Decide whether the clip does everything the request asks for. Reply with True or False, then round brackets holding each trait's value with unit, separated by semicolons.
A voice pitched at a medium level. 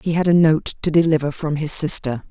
True (155 Hz)